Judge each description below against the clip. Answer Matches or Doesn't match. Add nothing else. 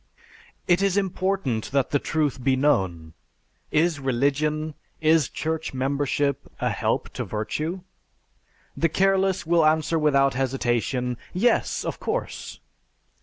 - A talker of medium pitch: Matches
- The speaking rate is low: Matches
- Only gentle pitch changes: Doesn't match